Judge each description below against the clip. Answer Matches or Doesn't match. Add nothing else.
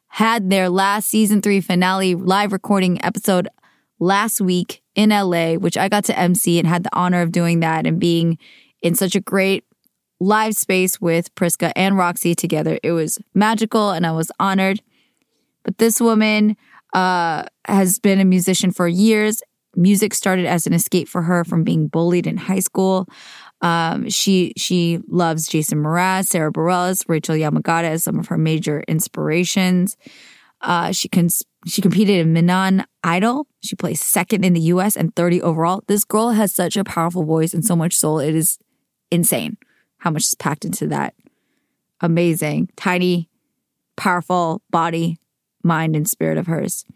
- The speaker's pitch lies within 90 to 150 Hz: Doesn't match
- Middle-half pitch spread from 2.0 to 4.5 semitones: Matches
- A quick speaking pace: Doesn't match